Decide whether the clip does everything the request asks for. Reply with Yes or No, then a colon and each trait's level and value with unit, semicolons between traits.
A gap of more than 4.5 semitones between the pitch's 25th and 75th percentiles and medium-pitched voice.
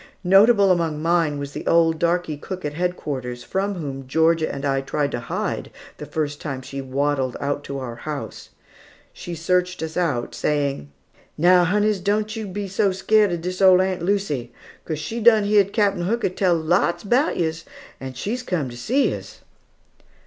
Yes: average, 5.1 semitones; medium, 170 Hz